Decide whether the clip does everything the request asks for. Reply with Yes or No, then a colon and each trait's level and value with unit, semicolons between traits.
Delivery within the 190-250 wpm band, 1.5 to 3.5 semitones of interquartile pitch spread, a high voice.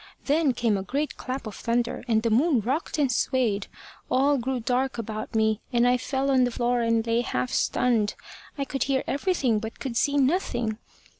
Yes: average, 195 wpm; average, 3.1 semitones; high, 245 Hz